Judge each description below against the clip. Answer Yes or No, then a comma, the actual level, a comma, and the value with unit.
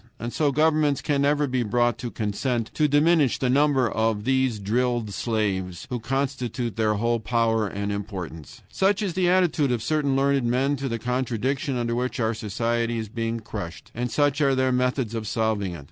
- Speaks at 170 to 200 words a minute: Yes, average, 190 wpm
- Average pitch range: Yes, average, 3.7 semitones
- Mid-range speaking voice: No, low, 120 Hz